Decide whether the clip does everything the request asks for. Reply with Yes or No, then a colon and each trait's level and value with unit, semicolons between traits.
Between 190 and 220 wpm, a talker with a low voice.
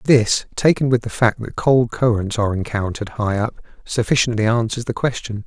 No: average, 175 wpm; low, 115 Hz